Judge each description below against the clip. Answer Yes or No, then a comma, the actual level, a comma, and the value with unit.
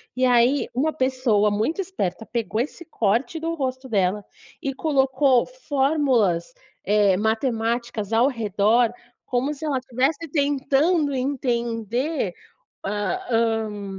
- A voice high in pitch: Yes, very high, 250 Hz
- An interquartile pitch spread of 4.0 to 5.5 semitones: Yes, average, 4.3 semitones